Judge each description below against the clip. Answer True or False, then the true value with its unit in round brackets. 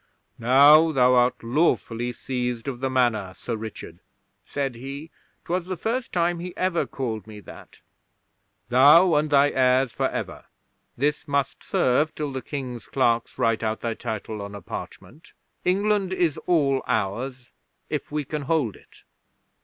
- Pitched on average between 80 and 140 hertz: True (135 Hz)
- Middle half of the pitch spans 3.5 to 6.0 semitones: True (4.6 semitones)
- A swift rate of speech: False (155 wpm)